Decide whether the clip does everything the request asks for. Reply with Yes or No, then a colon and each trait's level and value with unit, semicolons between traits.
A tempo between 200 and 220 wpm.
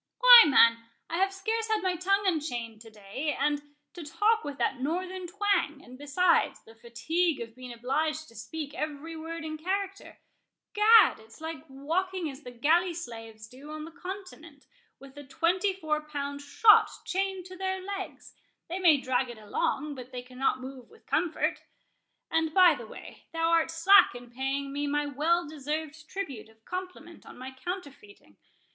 No: average, 170 wpm